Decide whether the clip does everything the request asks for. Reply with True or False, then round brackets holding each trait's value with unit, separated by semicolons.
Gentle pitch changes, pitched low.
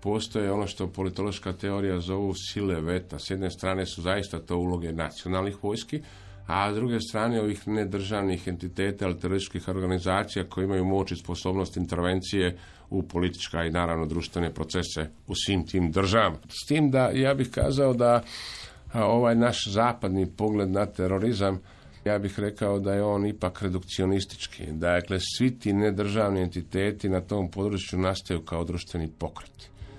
True (2.3 semitones; 95 Hz)